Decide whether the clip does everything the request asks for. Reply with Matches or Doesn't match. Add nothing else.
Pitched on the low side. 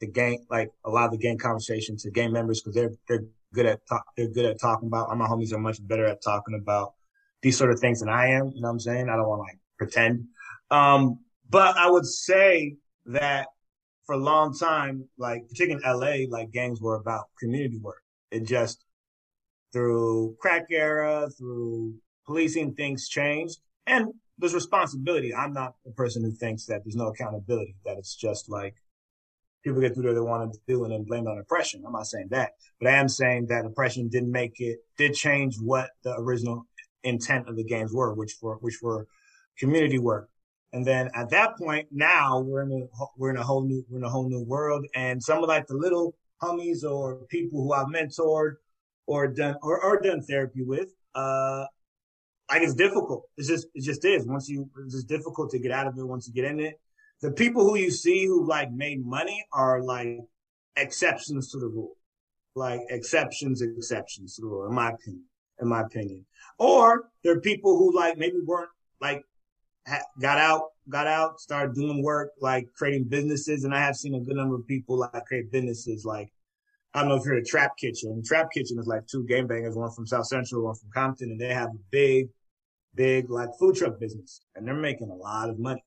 Matches